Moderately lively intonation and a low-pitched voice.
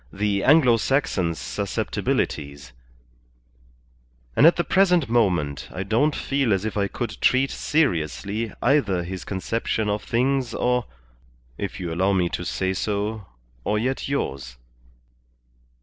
No: wide, 5.7 semitones; low, 105 Hz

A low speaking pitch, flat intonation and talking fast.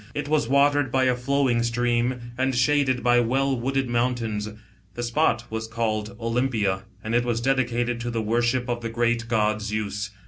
No: low, 120 Hz; narrow, 2.2 semitones; average, 175 wpm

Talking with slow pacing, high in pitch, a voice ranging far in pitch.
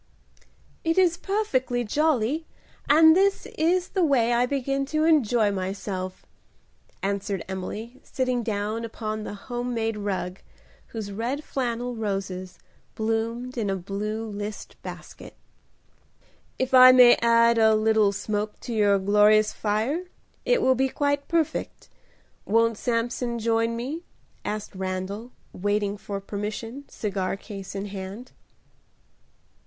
No: slow, 125 wpm; high, 225 Hz; average, 3.9 semitones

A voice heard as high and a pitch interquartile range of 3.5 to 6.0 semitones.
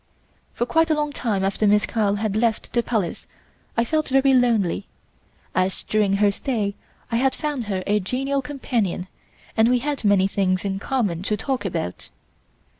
Yes: high, 220 Hz; average, 4.7 semitones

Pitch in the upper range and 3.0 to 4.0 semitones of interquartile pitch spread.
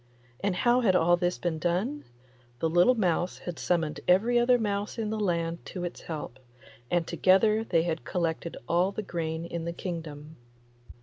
No: medium, 175 Hz; average, 3.6 semitones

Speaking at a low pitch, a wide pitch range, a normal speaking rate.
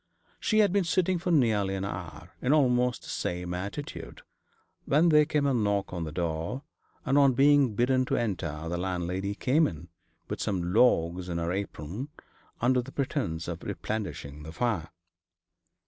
Yes: low, 100 Hz; wide, 7.8 semitones; average, 165 wpm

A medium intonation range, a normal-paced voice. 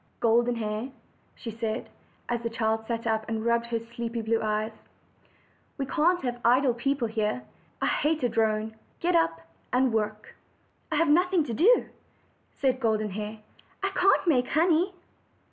Yes: average, 4.3 semitones; average, 160 wpm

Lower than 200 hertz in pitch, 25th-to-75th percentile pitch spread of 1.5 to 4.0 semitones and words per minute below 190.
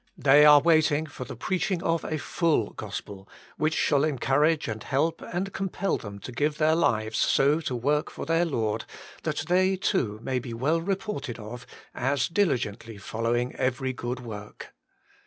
No: medium, 140 Hz; wide, 5.5 semitones; average, 165 wpm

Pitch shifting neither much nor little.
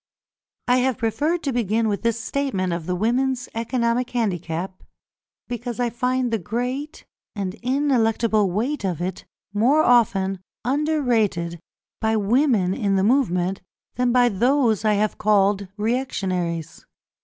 Yes: average, 4.4 semitones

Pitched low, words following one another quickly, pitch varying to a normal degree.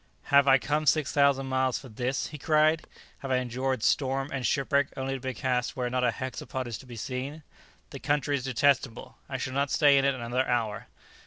No: low, 130 Hz; fast, 215 wpm; narrow, 1.8 semitones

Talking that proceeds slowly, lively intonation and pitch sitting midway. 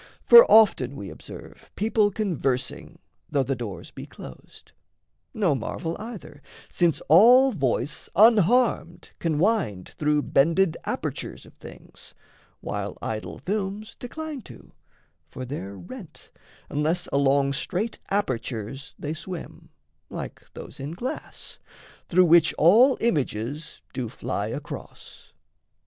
Yes: slow, 115 wpm; wide, 7.4 semitones; medium, 165 Hz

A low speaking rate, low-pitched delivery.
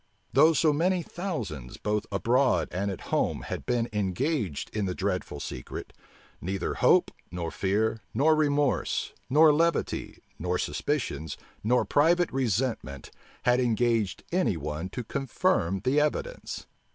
Yes: slow, 130 wpm; low, 115 Hz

